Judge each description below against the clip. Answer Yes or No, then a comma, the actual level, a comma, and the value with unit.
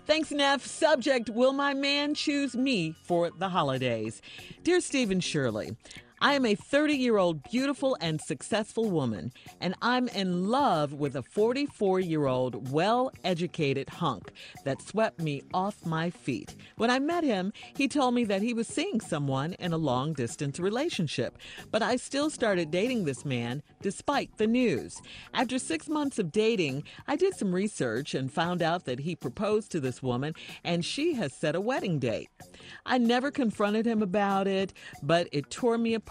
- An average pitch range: No, wide, 8.1 semitones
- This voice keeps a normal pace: Yes, average, 175 wpm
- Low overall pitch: No, high, 195 Hz